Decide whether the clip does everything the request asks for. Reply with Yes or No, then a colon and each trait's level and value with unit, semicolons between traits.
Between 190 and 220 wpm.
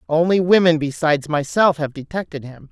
No: average, 155 wpm